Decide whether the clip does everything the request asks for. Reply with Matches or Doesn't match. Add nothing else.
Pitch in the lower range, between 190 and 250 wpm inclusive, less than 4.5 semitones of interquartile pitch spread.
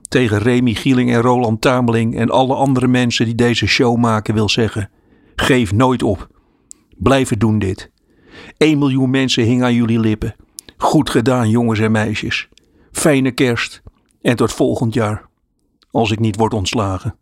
Doesn't match